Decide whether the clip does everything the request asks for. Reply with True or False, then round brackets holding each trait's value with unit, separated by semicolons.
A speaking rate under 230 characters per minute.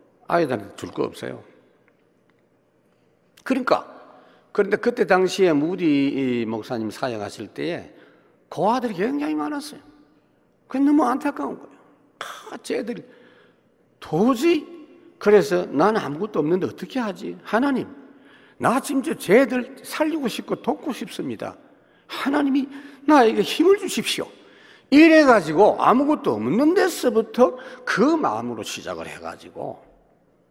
False (270 characters per minute)